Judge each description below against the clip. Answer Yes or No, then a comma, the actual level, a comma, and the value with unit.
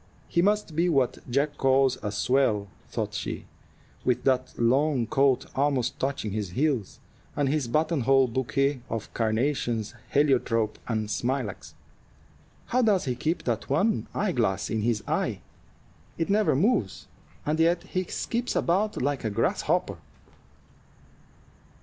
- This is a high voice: No, low, 135 Hz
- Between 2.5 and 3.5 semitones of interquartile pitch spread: No, average, 5.1 semitones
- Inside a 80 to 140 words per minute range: Yes, slow, 135 wpm